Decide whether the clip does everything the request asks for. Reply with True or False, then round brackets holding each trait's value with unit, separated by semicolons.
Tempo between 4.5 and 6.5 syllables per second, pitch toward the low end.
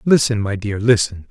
True (5.0 syllables/s; 110 Hz)